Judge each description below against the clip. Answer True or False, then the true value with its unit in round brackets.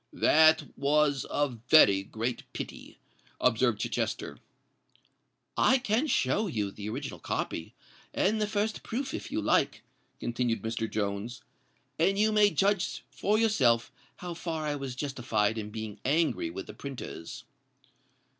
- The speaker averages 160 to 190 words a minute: False (140 wpm)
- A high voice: False (140 Hz)